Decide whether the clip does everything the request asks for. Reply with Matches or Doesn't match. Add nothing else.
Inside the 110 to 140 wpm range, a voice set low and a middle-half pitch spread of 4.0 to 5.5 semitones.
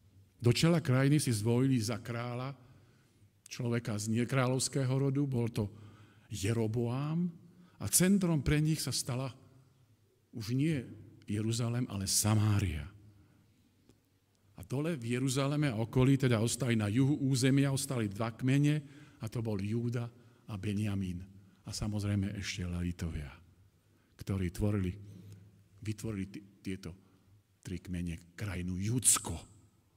Matches